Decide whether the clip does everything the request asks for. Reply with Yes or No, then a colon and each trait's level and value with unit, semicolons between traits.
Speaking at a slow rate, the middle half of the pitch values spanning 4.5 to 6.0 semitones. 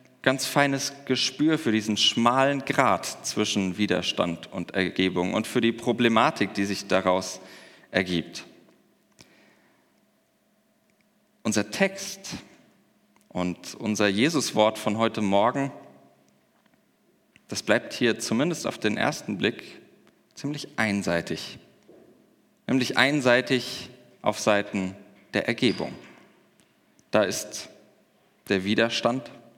Yes: slow, 95 wpm; average, 5.2 semitones